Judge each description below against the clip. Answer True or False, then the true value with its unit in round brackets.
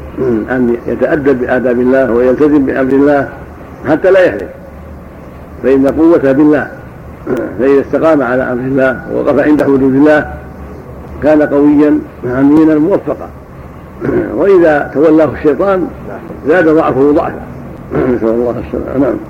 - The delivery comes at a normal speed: True (110 wpm)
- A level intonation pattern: False (4.1 semitones)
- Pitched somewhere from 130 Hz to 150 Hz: True (135 Hz)